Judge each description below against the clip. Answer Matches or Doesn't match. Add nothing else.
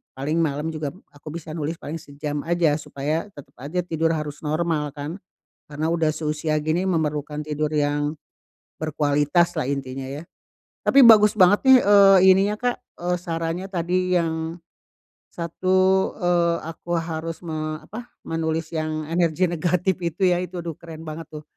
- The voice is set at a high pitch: Doesn't match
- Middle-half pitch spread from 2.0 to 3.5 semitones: Matches